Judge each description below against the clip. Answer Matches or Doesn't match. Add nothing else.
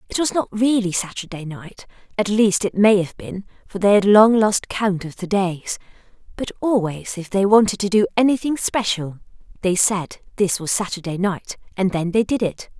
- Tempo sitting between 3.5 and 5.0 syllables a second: Matches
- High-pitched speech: Matches